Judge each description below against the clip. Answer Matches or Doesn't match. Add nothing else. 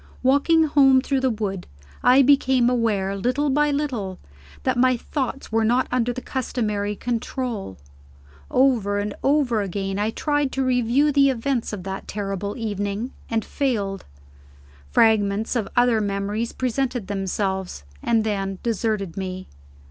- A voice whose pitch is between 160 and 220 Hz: Doesn't match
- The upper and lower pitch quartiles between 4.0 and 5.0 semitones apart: Matches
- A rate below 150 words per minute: Matches